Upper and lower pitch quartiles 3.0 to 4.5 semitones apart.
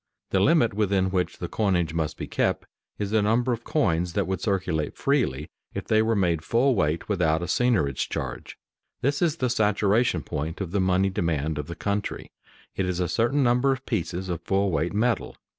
No: average, 5.3 semitones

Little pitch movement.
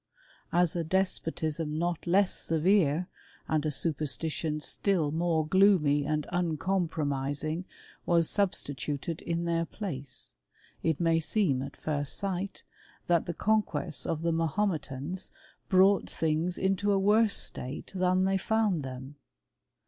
No: average, 3.7 semitones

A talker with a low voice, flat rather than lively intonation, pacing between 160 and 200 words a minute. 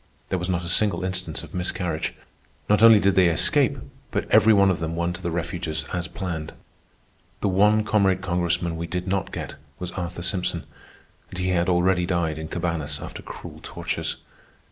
Yes: very low, 90 Hz; narrow, 1.8 semitones; average, 185 wpm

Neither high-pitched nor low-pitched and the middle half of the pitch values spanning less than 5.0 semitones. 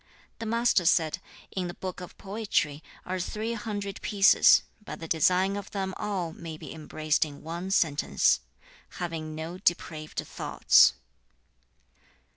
Yes: medium, 180 Hz; average, 3.8 semitones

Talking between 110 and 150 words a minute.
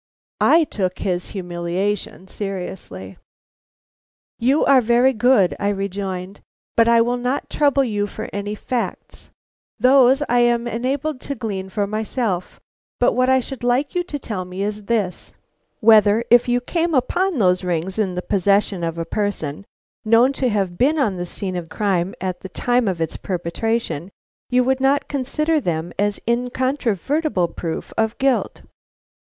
No: average, 160 wpm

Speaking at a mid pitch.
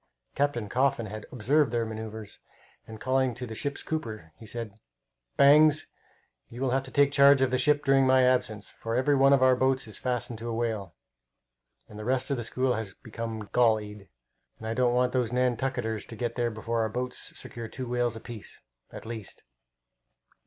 No: low, 120 Hz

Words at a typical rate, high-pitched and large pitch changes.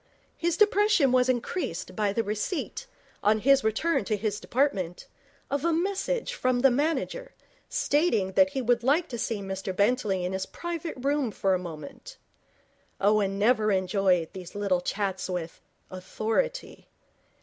Yes: average, 150 wpm; high, 220 Hz; wide, 7.0 semitones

